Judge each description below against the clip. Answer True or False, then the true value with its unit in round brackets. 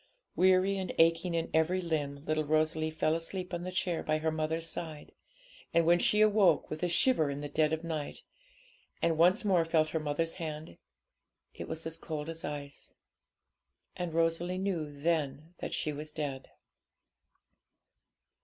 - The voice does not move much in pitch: True (2.1 semitones)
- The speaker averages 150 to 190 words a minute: True (165 wpm)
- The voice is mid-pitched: True (160 Hz)